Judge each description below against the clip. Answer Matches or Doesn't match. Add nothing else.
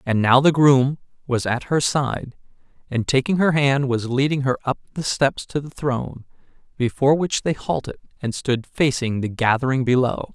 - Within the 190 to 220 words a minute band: Doesn't match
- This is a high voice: Doesn't match